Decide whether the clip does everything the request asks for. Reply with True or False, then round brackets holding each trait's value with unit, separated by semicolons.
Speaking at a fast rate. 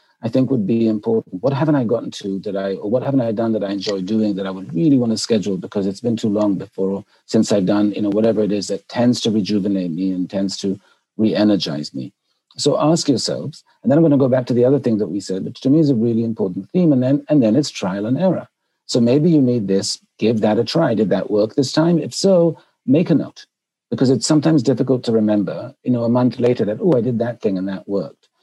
True (260 wpm)